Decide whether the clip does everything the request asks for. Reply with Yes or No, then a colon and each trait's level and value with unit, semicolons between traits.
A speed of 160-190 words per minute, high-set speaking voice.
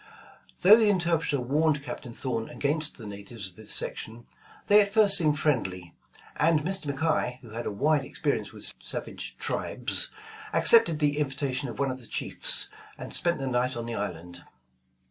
No: average, 170 wpm; medium, 140 Hz